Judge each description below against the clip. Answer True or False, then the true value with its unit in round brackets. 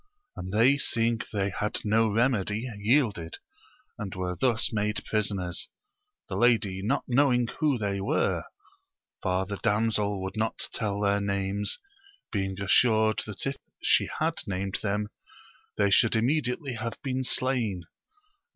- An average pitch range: True (3.2 semitones)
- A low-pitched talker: True (105 Hz)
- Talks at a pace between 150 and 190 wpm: False (140 wpm)